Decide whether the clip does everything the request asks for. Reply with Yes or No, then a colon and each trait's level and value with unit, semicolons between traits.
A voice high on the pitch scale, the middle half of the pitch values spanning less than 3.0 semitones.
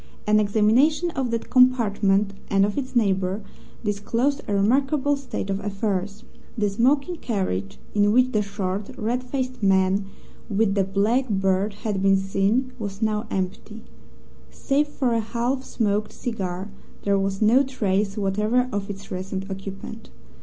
No: high, 210 Hz; average, 3.9 semitones